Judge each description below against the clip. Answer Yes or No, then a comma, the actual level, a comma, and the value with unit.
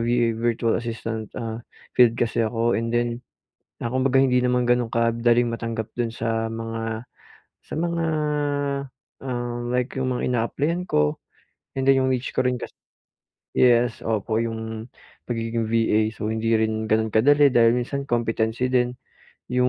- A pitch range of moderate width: No, narrow, 1.8 semitones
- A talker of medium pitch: No, low, 115 Hz